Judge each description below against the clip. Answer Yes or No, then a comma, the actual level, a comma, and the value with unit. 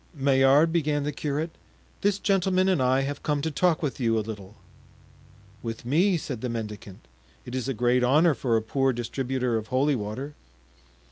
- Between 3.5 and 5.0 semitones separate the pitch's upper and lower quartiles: Yes, average, 4.3 semitones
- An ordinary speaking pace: Yes, average, 180 wpm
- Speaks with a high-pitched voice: No, low, 135 Hz